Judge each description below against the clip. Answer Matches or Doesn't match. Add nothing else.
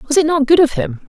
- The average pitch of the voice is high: Matches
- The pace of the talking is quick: Matches